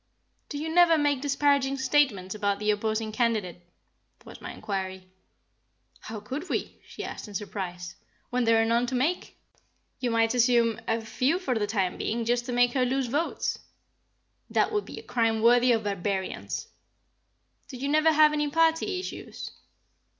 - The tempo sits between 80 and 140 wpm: No, average, 165 wpm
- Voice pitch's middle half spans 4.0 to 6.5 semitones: Yes, average, 5.0 semitones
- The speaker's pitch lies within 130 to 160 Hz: No, high, 240 Hz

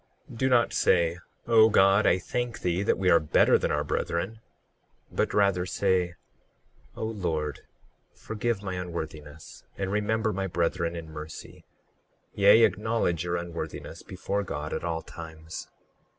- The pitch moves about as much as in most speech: Yes, average, 3.8 semitones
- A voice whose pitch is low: Yes, very low, 90 Hz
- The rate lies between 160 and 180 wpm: No, average, 140 wpm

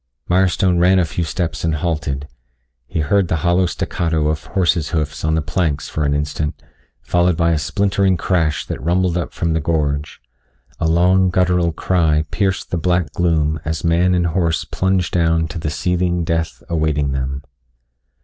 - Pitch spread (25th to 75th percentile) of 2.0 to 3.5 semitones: Yes, narrow, 2.5 semitones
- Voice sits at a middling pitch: No, very low, 85 Hz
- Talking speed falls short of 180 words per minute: Yes, average, 170 wpm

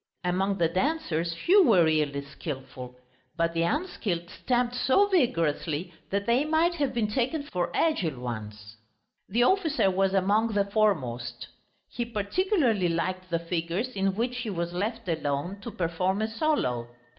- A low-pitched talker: No, high, 195 Hz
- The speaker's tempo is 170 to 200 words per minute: No, average, 150 wpm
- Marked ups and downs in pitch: Yes, wide, 6.5 semitones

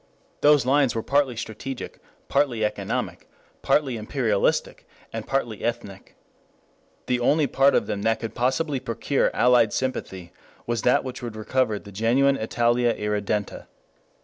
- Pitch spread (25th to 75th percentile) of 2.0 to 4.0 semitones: Yes, average, 3.5 semitones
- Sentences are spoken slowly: Yes, slow, 130 wpm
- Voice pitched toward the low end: Yes, low, 120 Hz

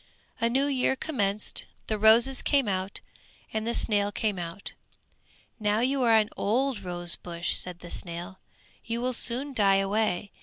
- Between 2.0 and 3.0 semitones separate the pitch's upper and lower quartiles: No, average, 3.9 semitones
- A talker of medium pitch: No, high, 215 Hz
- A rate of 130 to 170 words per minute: Yes, average, 160 wpm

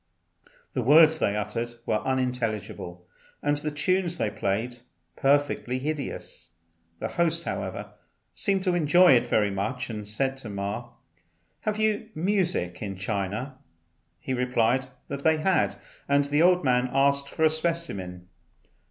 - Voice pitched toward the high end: No, low, 135 Hz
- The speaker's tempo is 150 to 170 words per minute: No, average, 140 wpm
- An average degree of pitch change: No, wide, 6.6 semitones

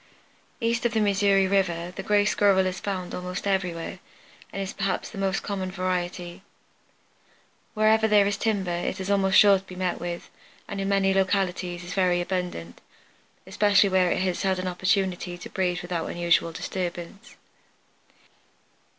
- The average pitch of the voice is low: No, high, 190 Hz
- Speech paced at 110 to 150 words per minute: No, average, 160 wpm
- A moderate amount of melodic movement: No, narrow, 1.9 semitones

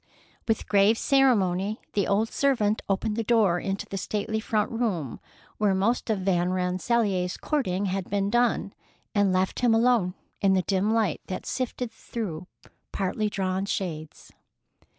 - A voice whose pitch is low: No, high, 200 Hz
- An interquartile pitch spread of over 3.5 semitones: No, average, 3.2 semitones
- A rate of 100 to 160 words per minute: Yes, average, 150 wpm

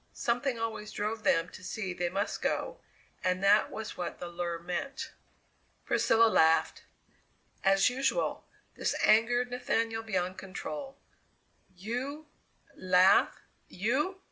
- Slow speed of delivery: Yes, slow, 115 wpm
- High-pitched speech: Yes, high, 215 Hz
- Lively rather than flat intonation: No, average, 4.9 semitones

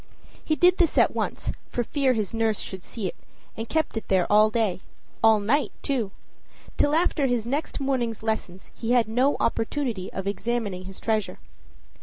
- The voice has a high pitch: Yes, high, 225 Hz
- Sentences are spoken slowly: No, average, 175 wpm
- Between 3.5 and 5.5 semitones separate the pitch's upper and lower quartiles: Yes, average, 4.3 semitones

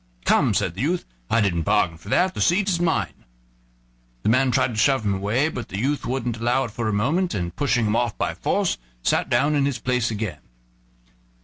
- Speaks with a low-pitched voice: Yes, low, 120 Hz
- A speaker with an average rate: No, fast, 215 wpm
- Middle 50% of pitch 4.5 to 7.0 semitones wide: Yes, average, 5.1 semitones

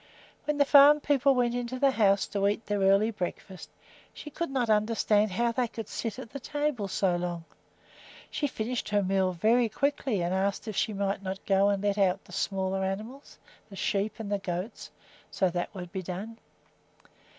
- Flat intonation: No, average, 3.8 semitones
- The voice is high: Yes, high, 205 Hz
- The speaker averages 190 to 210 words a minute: Yes, average, 195 wpm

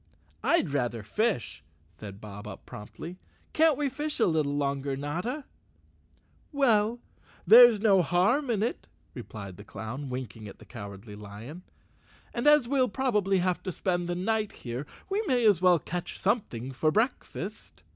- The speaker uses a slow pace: No, average, 155 wpm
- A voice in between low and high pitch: Yes, medium, 175 Hz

